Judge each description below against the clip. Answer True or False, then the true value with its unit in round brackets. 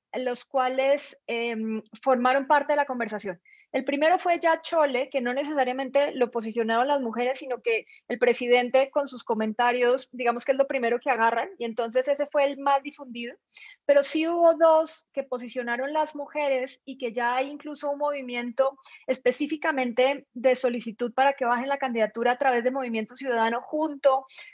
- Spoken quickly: False (170 wpm)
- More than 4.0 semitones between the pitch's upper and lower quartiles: False (2.8 semitones)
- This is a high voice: True (260 Hz)